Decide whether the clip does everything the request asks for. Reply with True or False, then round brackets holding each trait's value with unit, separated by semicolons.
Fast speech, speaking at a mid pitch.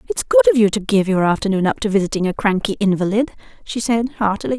False (225 wpm; 210 Hz)